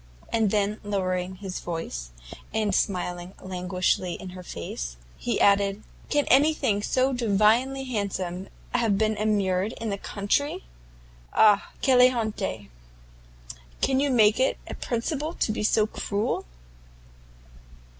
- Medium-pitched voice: No, high, 205 Hz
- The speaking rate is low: Yes, slow, 125 wpm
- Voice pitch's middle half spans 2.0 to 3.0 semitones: No, average, 3.8 semitones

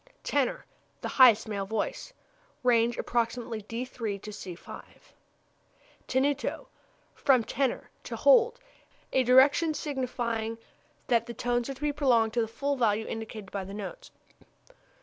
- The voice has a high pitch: Yes, high, 240 Hz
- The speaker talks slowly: Yes, slow, 130 wpm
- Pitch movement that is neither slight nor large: Yes, average, 3.3 semitones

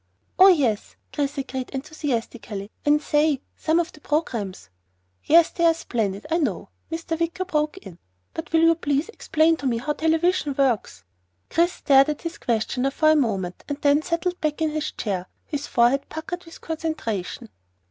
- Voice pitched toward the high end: Yes, very high, 295 Hz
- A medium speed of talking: Yes, average, 175 wpm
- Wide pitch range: No, average, 5.0 semitones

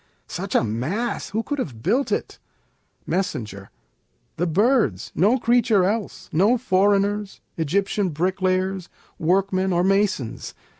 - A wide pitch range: No, average, 3.7 semitones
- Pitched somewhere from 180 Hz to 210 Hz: Yes, high, 190 Hz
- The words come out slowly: Yes, slow, 115 wpm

